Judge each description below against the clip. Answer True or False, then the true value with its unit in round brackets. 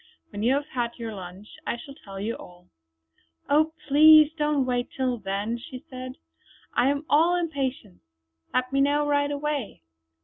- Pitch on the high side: True (260 Hz)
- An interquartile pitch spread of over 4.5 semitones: False (4.0 semitones)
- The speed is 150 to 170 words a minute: True (165 wpm)